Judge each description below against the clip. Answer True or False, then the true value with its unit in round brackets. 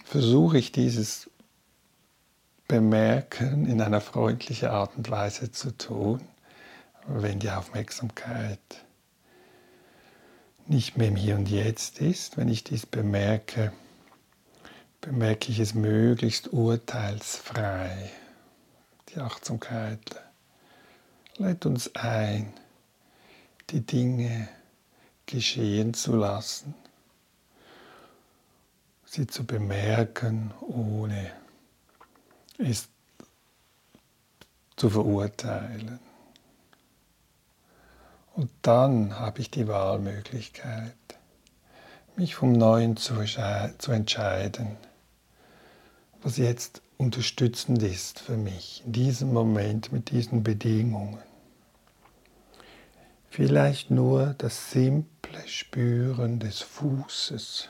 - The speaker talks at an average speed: False (80 wpm)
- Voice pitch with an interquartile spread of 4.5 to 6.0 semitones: False (2.7 semitones)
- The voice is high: False (115 Hz)